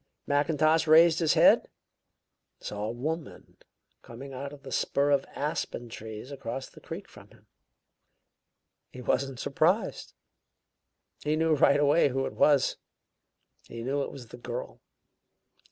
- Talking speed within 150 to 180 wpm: No, average, 140 wpm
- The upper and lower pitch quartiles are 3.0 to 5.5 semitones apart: Yes, average, 3.4 semitones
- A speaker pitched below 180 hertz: Yes, medium, 140 Hz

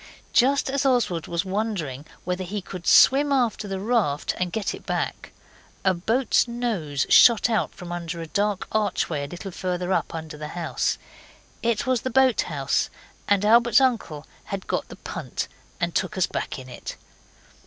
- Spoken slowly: No, average, 170 wpm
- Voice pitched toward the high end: Yes, high, 195 Hz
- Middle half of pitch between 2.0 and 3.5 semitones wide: No, wide, 5.4 semitones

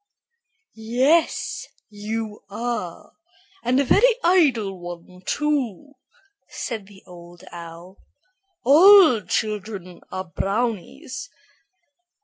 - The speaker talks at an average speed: No, slow, 85 wpm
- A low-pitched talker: No, high, 220 Hz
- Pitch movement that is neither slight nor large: No, wide, 6.4 semitones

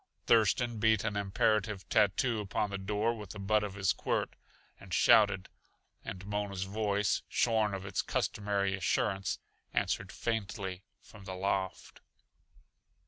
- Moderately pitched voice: No, low, 100 Hz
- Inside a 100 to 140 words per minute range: Yes, slow, 135 wpm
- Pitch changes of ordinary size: No, narrow, 1.9 semitones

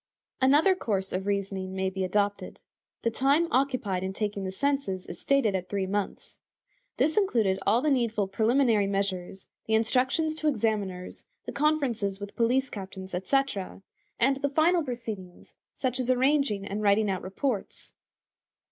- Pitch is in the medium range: No, high, 215 Hz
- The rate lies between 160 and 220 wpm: No, average, 150 wpm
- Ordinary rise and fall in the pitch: No, wide, 5.8 semitones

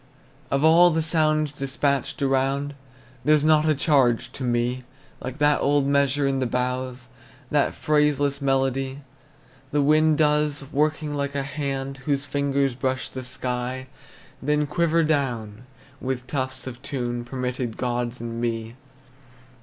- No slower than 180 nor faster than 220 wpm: No, average, 140 wpm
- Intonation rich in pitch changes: No, narrow, 2.6 semitones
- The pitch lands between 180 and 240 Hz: No, low, 135 Hz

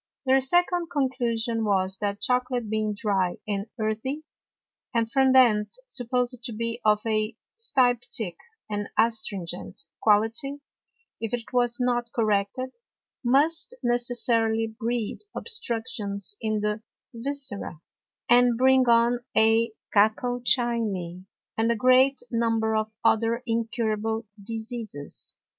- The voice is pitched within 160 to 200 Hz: No, high, 230 Hz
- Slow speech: Yes, slow, 110 wpm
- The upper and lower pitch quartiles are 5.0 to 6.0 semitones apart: No, narrow, 2.5 semitones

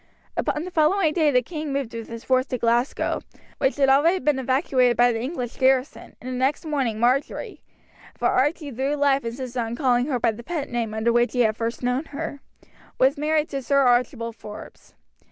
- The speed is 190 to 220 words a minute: Yes, average, 200 wpm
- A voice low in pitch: No, very high, 260 Hz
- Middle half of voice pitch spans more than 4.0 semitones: No, average, 3.3 semitones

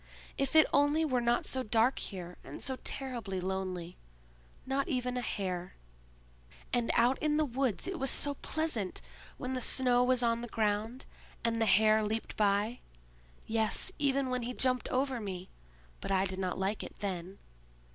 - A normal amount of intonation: Yes, average, 4.6 semitones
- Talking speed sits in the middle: Yes, average, 165 wpm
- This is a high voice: Yes, high, 235 Hz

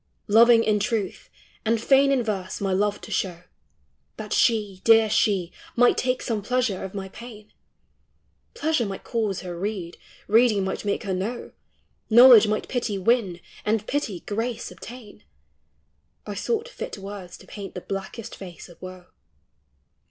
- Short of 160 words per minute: No, average, 165 wpm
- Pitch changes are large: No, average, 3.6 semitones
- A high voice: Yes, high, 210 Hz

